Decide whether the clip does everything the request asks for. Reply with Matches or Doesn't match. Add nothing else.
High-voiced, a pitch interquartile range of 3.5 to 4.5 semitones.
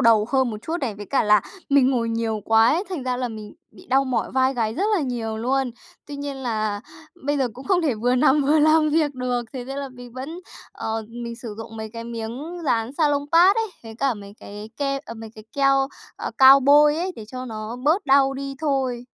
Matches